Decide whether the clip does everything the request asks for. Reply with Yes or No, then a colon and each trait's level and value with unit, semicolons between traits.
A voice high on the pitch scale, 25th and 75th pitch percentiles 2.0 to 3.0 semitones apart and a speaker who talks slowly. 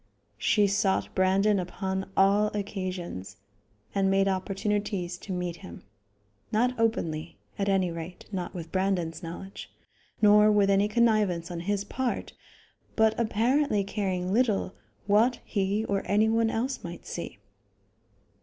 Yes: high, 195 Hz; narrow, 2.5 semitones; slow, 130 wpm